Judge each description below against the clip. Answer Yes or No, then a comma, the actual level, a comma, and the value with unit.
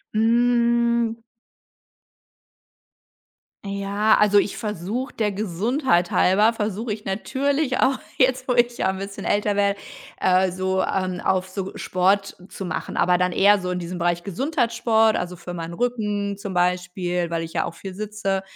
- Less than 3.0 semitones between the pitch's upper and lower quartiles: No, average, 3.9 semitones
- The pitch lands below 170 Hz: No, high, 200 Hz